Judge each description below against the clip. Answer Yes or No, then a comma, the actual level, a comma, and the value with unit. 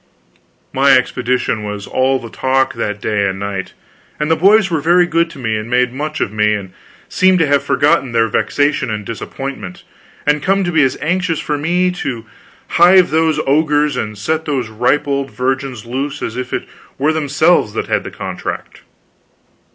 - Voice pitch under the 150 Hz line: Yes, low, 135 Hz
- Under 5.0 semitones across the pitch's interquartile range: No, wide, 5.4 semitones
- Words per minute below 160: No, average, 185 wpm